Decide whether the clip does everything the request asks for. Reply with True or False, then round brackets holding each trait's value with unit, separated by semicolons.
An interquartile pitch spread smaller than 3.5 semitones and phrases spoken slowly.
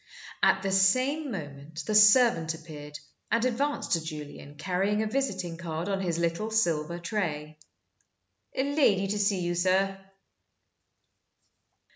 False (4.7 semitones; 130 wpm)